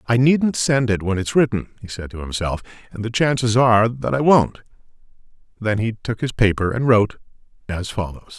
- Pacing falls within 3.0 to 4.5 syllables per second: No, 5.4 syllables/s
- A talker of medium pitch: No, low, 115 Hz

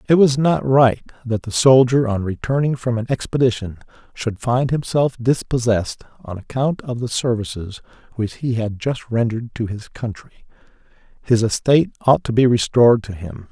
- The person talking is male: Yes, male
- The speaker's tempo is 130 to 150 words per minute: No, average, 165 wpm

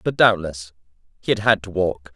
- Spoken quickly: No, average, 195 wpm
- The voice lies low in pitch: Yes, very low, 95 Hz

